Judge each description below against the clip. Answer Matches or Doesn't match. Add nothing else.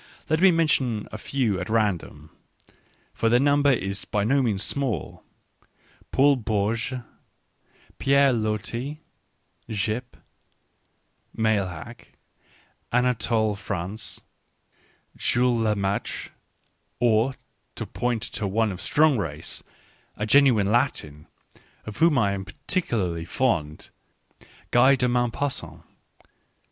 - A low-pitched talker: Matches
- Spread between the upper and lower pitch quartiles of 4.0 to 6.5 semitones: Matches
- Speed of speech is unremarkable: Doesn't match